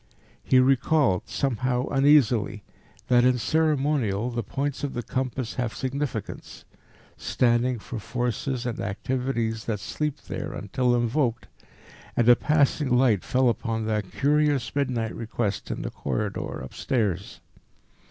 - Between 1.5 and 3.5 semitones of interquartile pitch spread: Yes, average, 3.2 semitones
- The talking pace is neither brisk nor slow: No, slow, 125 wpm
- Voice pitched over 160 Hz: No, low, 125 Hz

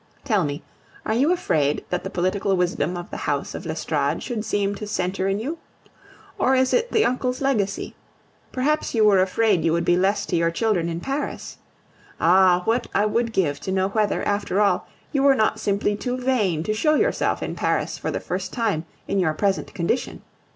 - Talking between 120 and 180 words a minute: No, average, 200 wpm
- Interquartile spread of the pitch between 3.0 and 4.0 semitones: No, average, 5.1 semitones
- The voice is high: Yes, high, 205 Hz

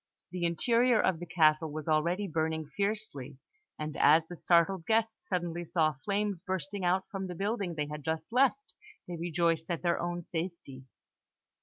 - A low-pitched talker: No, medium, 170 Hz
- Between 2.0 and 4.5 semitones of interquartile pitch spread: Yes, average, 3.5 semitones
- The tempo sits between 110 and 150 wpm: No, average, 165 wpm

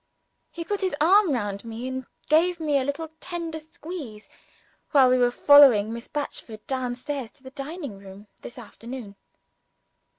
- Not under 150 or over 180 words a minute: Yes, average, 155 wpm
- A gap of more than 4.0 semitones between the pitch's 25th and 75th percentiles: Yes, average, 5.3 semitones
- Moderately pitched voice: No, very high, 265 Hz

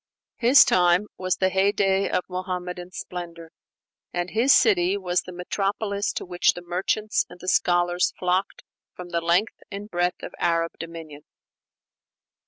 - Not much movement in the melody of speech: Yes, narrow, 1.9 semitones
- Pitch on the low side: No, medium, 180 Hz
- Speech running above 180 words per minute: No, average, 145 wpm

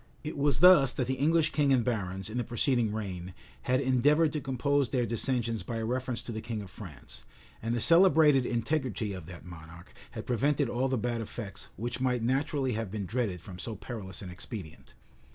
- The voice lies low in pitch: Yes, low, 120 Hz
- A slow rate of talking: No, average, 200 wpm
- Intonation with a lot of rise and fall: No, average, 4.2 semitones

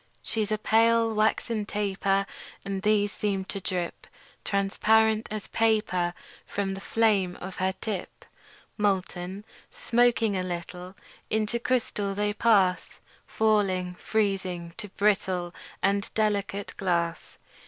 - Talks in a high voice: Yes, high, 200 Hz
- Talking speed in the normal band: No, slow, 115 wpm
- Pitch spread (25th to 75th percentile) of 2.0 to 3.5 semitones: Yes, narrow, 2.5 semitones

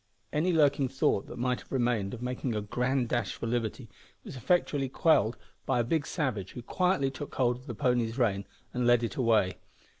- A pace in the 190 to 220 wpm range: Yes, average, 200 wpm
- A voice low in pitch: Yes, low, 125 Hz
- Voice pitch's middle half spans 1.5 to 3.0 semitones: Yes, average, 2.7 semitones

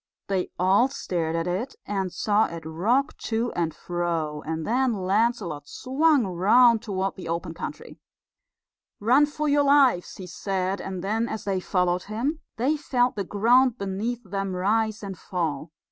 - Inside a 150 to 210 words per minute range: Yes, average, 160 wpm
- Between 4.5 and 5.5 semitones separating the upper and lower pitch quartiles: Yes, average, 5.2 semitones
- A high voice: Yes, high, 200 Hz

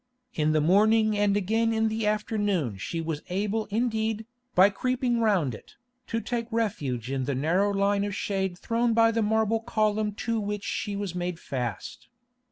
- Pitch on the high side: Yes, high, 205 Hz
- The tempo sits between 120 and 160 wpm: No, average, 175 wpm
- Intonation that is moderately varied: Yes, average, 3.9 semitones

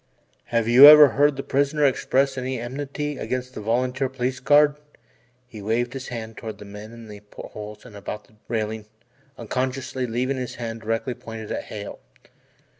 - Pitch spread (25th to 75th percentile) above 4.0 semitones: No, average, 3.2 semitones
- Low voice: Yes, low, 125 Hz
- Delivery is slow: No, average, 170 wpm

